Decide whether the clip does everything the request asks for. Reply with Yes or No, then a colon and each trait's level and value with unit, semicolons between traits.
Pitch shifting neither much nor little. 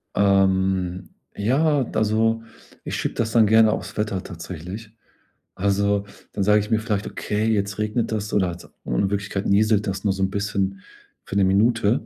No: narrow, 2.0 semitones